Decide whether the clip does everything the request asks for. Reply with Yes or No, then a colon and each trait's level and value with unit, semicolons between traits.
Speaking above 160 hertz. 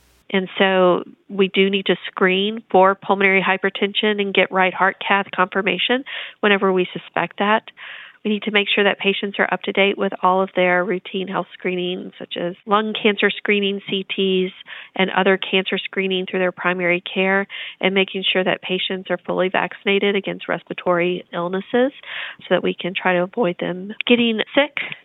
Yes: high, 190 Hz